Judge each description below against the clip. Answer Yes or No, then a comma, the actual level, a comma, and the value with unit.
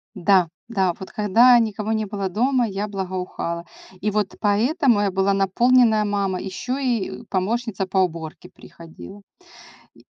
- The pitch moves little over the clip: No, average, 3.3 semitones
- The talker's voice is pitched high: Yes, high, 205 Hz